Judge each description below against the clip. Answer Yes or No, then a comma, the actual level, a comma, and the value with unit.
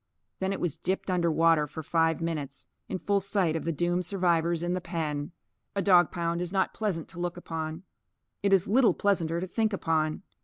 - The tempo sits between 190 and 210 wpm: Yes, average, 200 wpm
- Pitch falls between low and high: Yes, medium, 175 Hz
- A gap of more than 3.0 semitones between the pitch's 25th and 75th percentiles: No, narrow, 2.6 semitones